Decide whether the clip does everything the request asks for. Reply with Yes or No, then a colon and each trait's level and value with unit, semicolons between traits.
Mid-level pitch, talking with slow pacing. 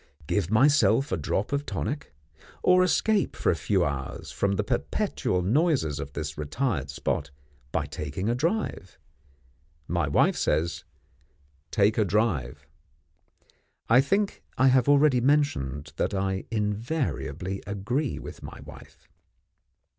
No: low, 105 Hz; slow, 130 wpm